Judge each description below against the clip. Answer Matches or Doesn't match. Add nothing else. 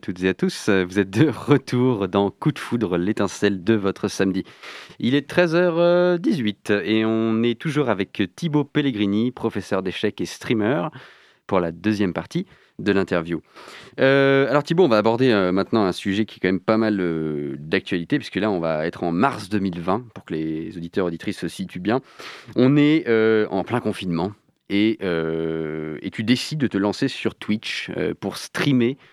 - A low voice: Matches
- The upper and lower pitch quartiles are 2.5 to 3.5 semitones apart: Doesn't match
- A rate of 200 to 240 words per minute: Doesn't match